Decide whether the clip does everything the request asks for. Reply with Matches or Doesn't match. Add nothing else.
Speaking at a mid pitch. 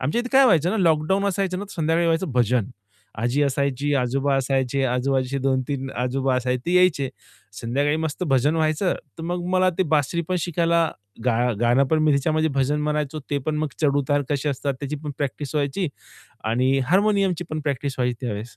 Matches